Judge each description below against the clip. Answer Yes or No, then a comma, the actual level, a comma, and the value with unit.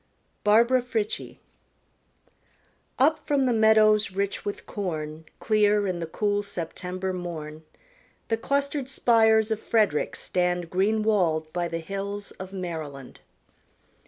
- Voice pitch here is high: Yes, high, 200 Hz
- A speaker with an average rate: No, slow, 125 wpm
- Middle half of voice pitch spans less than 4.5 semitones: Yes, average, 4.0 semitones